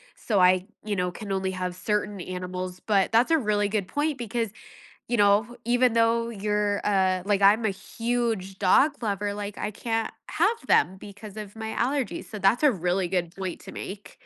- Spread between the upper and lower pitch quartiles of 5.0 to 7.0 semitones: No, average, 3.2 semitones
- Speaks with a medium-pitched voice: No, high, 205 Hz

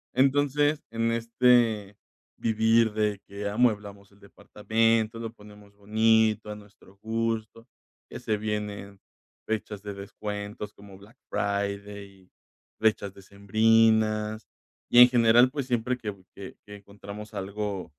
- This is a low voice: Yes, low, 105 Hz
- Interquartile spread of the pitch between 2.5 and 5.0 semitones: No, narrow, 2.0 semitones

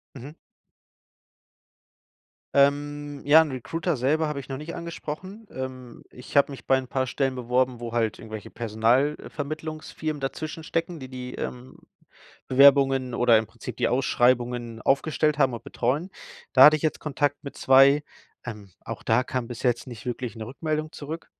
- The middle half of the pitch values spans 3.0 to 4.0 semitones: Yes, average, 3.5 semitones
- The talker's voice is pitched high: No, low, 135 Hz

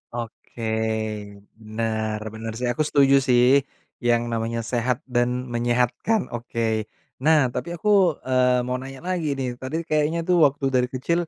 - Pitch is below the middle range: Yes, low, 125 Hz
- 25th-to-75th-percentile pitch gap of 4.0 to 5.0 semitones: No, average, 3.0 semitones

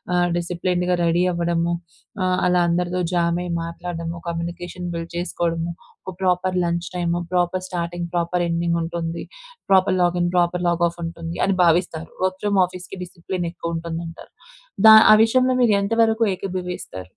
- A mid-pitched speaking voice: Yes, medium, 175 Hz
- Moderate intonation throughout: No, narrow, 1.3 semitones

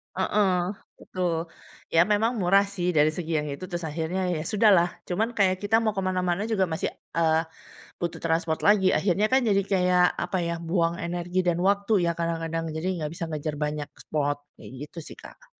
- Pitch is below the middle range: No, medium, 175 Hz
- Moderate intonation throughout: Yes, average, 3.0 semitones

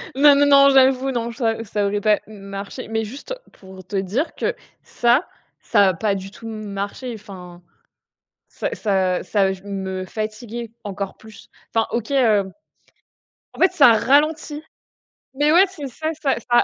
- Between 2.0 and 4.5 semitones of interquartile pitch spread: No, average, 5.3 semitones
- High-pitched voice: Yes, high, 220 Hz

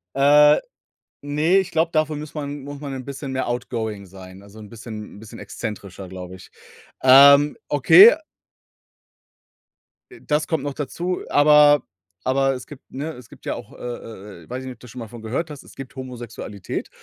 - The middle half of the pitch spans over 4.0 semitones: Yes, average, 4.9 semitones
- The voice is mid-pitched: No, low, 130 Hz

